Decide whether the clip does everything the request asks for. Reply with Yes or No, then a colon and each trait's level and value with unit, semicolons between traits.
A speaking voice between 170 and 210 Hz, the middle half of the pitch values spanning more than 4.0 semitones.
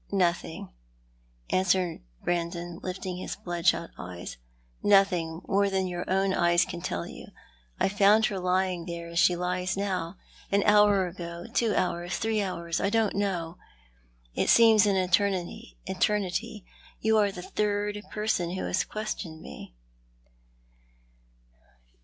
No: medium, 185 Hz; average, 2.7 semitones